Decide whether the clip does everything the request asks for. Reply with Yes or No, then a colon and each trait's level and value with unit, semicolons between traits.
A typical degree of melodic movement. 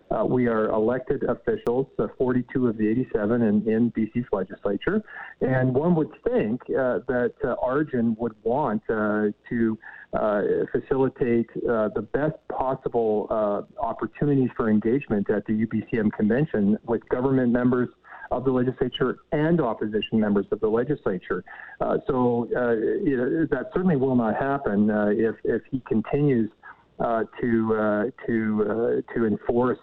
Yes: average, 3.5 semitones